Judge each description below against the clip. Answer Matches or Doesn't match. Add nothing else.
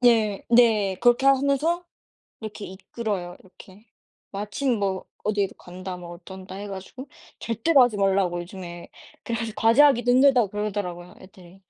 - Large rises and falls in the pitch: Doesn't match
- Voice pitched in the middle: Doesn't match